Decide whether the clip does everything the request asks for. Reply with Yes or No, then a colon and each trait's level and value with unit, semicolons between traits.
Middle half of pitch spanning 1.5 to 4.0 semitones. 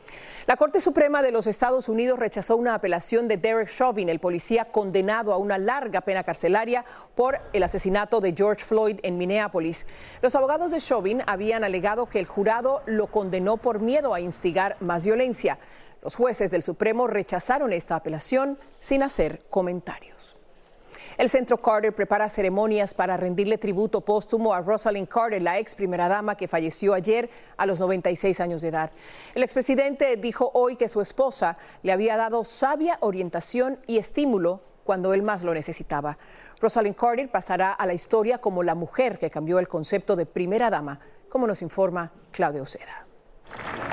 No: average, 4.4 semitones